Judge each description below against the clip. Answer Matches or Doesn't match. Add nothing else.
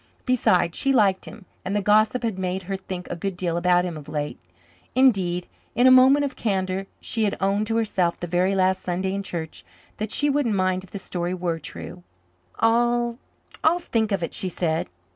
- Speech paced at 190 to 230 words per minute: Matches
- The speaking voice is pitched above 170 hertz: Matches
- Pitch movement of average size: Matches